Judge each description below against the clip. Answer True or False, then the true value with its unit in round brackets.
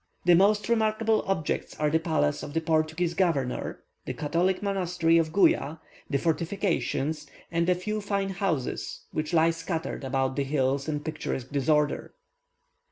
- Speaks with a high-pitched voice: False (165 Hz)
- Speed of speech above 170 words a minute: False (150 wpm)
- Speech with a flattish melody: False (4.2 semitones)